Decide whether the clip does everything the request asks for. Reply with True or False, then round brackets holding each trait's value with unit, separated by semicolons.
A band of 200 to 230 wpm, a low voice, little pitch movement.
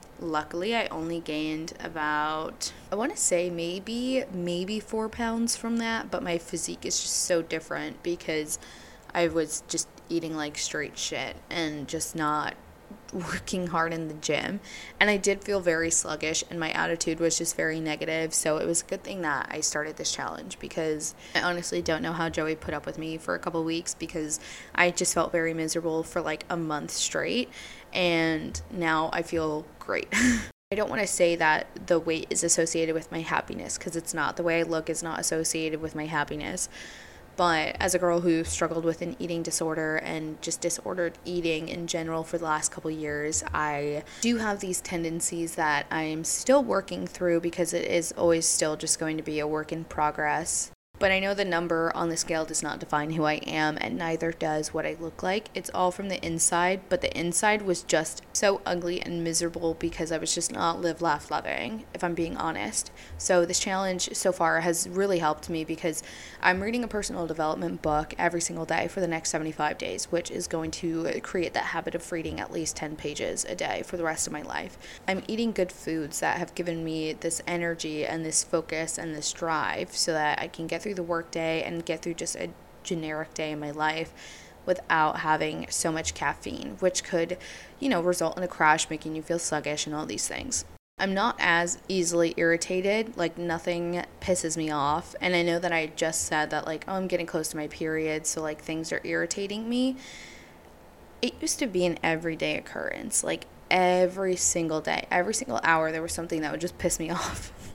False (205 wpm; 165 Hz; 1.9 semitones)